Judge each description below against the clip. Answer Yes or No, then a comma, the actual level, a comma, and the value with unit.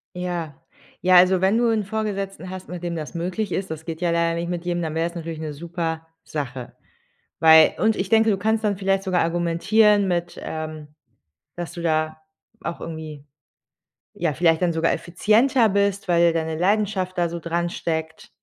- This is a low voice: No, medium, 175 Hz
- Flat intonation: No, average, 3.0 semitones